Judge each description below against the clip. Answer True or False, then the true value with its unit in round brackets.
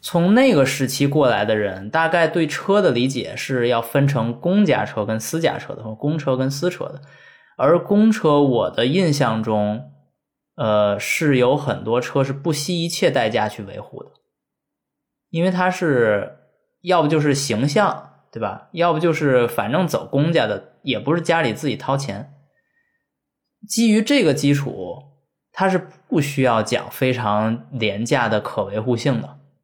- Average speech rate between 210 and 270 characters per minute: True (225 characters per minute)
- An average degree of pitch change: False (5.8 semitones)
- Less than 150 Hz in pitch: True (140 Hz)